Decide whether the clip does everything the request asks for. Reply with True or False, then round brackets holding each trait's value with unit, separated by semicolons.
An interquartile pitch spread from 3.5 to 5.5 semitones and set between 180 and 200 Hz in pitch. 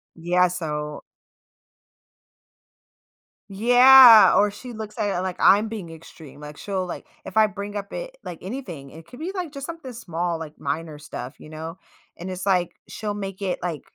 True (5.1 semitones; 185 Hz)